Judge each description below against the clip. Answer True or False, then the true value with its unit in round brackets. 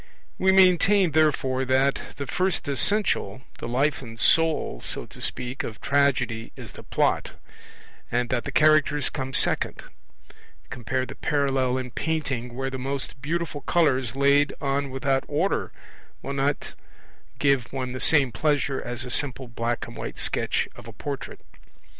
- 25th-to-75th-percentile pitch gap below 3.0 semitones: True (2.6 semitones)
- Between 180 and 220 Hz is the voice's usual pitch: False (135 Hz)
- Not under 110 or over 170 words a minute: True (155 wpm)